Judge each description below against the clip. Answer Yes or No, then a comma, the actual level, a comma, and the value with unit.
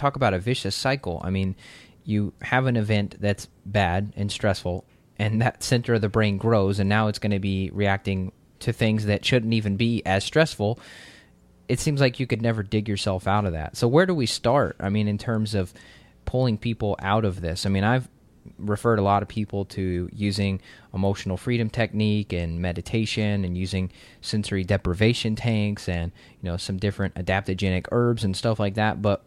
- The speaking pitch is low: Yes, low, 105 Hz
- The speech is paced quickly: No, average, 195 wpm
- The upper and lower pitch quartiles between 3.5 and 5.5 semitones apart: No, average, 2.9 semitones